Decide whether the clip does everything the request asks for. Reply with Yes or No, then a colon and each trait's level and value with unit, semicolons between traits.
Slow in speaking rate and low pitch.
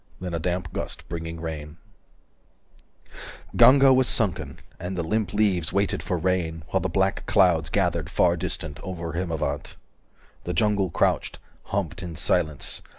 No: average, 150 wpm; very low, 90 Hz